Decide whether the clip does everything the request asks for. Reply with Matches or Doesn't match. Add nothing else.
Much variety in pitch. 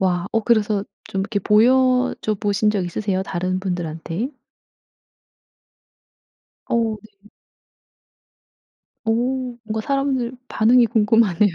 Doesn't match